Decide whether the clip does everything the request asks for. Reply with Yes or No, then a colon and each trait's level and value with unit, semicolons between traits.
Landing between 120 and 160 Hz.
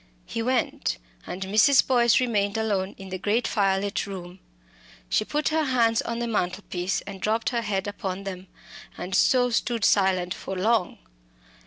No: high, 205 Hz